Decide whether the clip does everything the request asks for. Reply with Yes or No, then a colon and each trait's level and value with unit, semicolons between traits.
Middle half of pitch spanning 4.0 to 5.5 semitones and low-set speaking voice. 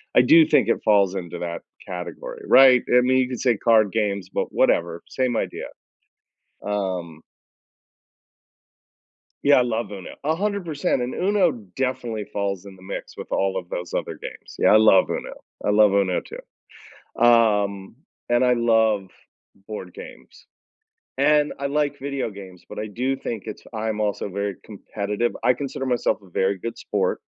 Yes: average, 4.6 semitones; low, 110 Hz